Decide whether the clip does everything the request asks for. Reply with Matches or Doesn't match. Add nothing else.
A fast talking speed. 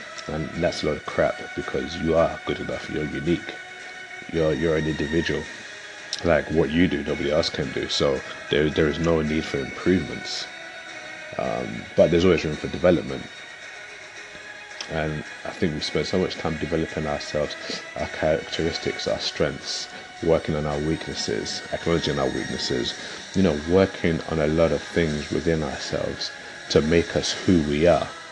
Doesn't match